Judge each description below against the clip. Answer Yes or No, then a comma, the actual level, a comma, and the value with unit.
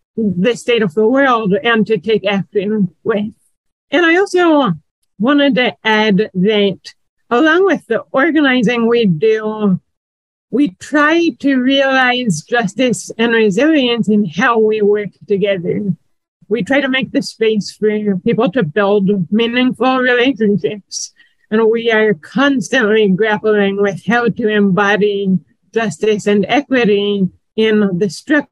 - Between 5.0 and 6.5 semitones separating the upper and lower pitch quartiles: No, average, 3.5 semitones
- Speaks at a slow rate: Yes, slow, 130 wpm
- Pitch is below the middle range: No, high, 215 Hz